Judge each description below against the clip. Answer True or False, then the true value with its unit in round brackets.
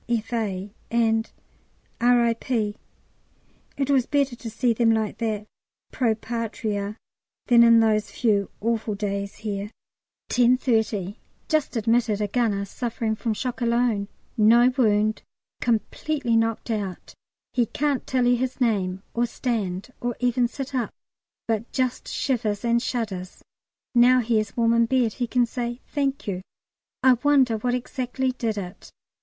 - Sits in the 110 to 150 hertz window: False (230 Hz)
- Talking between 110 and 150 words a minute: True (140 wpm)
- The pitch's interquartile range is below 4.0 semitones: True (2.5 semitones)